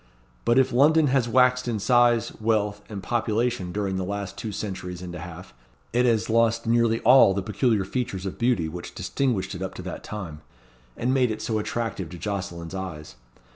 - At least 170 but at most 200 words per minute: Yes, average, 190 wpm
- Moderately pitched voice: No, low, 105 Hz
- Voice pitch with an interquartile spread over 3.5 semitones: Yes, average, 4.1 semitones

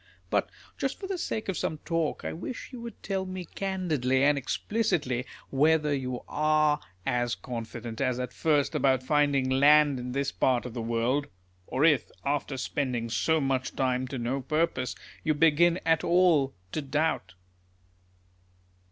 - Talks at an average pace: Yes, average, 160 wpm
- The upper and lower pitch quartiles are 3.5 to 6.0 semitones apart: Yes, average, 4.0 semitones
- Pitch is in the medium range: Yes, medium, 145 Hz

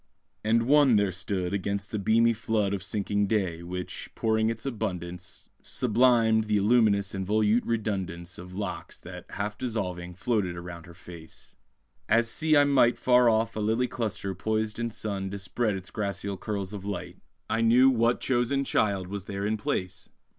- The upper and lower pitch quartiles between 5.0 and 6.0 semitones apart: No, average, 3.4 semitones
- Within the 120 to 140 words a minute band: No, average, 170 wpm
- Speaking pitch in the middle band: No, low, 105 Hz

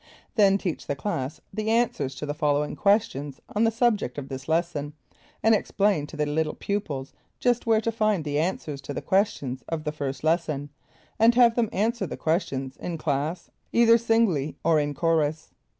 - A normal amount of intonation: No, wide, 6.7 semitones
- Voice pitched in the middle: Yes, medium, 165 Hz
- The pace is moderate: Yes, average, 180 wpm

